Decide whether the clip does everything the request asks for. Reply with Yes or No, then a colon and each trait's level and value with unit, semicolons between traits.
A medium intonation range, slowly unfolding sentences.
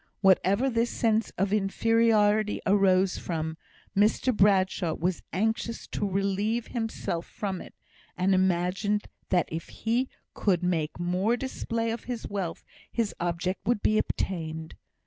Yes: average, 3.6 semitones; slow, 130 wpm